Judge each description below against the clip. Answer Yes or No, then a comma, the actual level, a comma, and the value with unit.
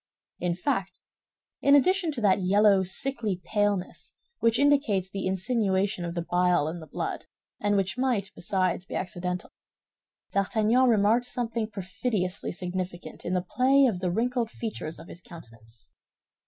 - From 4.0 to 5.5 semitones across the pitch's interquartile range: Yes, average, 4.3 semitones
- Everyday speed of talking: Yes, average, 145 wpm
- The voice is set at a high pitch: Yes, high, 195 Hz